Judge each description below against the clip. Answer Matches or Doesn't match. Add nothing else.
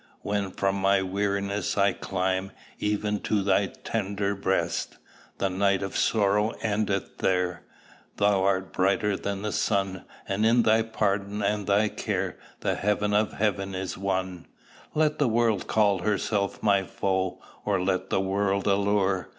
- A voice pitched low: Matches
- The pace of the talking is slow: Doesn't match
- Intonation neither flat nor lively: Doesn't match